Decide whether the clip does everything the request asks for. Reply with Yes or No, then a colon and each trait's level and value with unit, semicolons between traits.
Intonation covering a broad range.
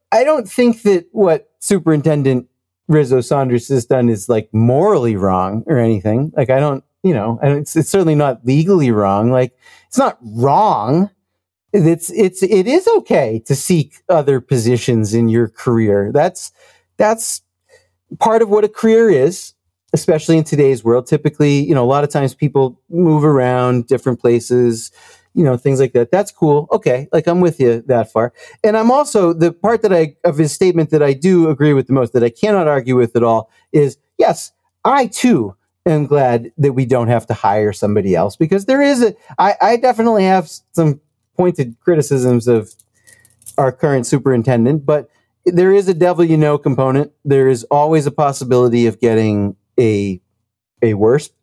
Yes: wide, 6.0 semitones